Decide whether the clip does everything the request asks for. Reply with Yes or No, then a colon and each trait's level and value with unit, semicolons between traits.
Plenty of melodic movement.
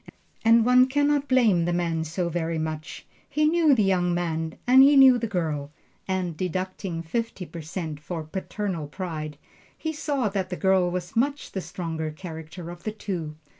Yes: wide, 5.9 semitones